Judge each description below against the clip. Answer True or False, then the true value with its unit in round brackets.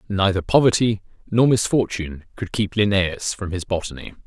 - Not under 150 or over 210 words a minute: False (140 wpm)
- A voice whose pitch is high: False (100 Hz)